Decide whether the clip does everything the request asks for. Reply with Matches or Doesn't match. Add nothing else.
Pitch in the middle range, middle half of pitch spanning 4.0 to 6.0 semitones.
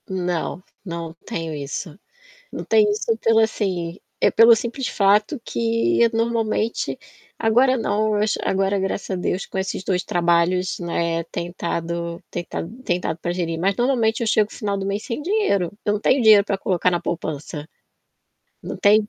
Doesn't match